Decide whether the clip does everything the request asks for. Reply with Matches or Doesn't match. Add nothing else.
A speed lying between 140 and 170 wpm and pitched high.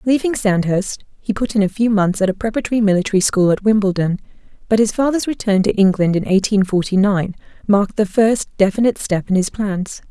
Doesn't match